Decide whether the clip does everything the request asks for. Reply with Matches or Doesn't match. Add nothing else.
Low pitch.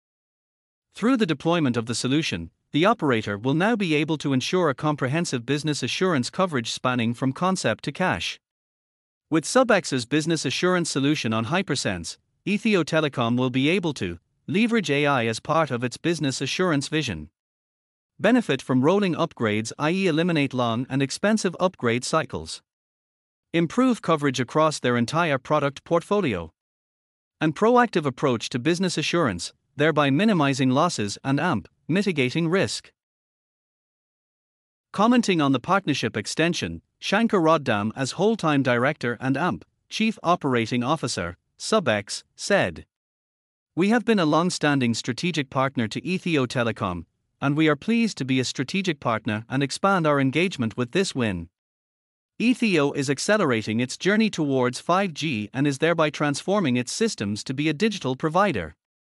Doesn't match